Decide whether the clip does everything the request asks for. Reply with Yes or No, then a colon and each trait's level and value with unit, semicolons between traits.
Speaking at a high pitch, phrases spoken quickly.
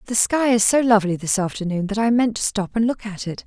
Yes: high, 215 Hz; fast, 275 wpm